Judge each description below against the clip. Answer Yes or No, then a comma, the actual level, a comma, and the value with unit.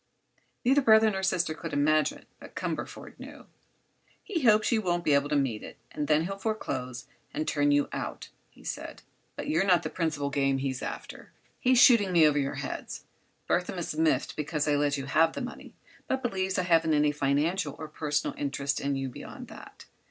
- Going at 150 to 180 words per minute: No, average, 195 wpm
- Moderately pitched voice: Yes, medium, 155 Hz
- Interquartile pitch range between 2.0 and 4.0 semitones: No, average, 4.8 semitones